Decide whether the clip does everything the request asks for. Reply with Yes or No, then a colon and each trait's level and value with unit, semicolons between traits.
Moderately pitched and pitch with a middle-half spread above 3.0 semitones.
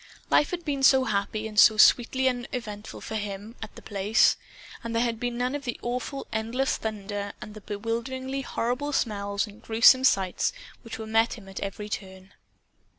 No: high, 225 Hz; average, 3.4 semitones